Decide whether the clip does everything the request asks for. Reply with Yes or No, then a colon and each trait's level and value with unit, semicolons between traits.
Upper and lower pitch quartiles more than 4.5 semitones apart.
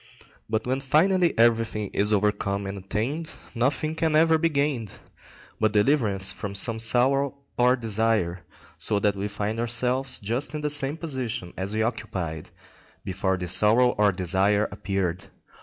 Yes: average, 5.0 semitones